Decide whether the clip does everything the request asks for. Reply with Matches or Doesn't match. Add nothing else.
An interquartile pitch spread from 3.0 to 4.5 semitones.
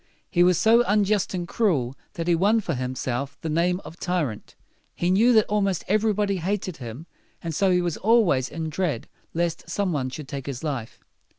Doesn't match